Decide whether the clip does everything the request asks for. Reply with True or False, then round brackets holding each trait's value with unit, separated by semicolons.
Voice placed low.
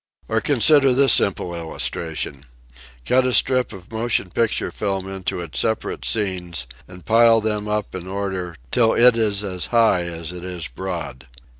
True (100 Hz)